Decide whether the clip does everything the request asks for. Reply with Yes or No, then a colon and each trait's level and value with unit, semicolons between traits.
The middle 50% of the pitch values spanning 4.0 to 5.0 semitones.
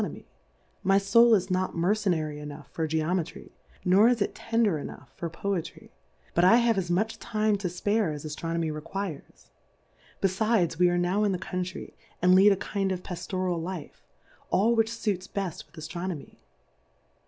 No: average, 3.4 semitones